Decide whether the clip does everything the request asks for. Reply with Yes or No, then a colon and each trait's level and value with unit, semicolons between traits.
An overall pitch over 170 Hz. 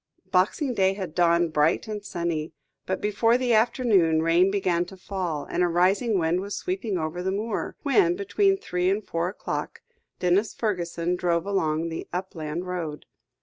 Yes: medium, 185 Hz